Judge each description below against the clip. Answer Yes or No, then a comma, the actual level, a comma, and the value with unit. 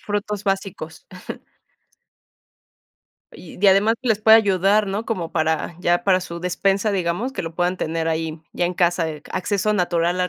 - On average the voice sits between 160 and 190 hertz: Yes, medium, 185 Hz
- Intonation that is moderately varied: Yes, average, 3.2 semitones